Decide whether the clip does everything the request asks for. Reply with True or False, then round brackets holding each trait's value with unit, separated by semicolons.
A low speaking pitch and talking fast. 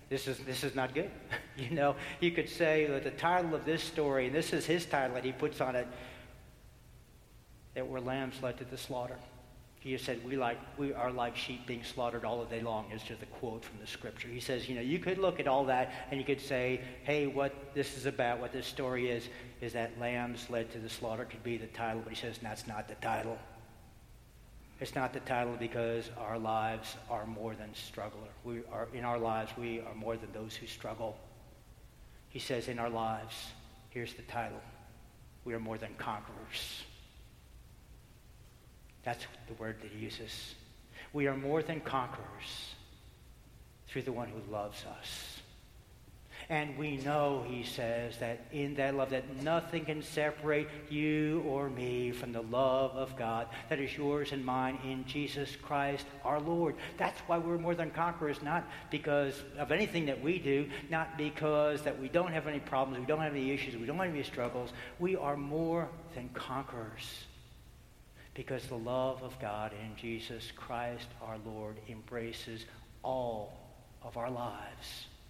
False (125 Hz; 185 wpm)